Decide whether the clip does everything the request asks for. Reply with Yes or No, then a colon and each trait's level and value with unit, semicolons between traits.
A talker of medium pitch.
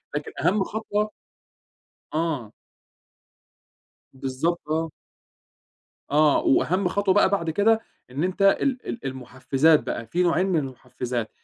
Yes: medium, 165 Hz